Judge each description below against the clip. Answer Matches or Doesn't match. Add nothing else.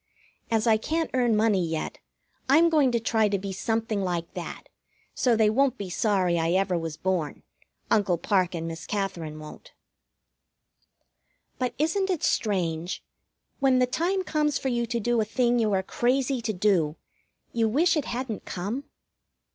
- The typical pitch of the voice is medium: Doesn't match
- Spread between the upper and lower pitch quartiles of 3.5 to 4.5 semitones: Doesn't match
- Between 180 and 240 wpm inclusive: Doesn't match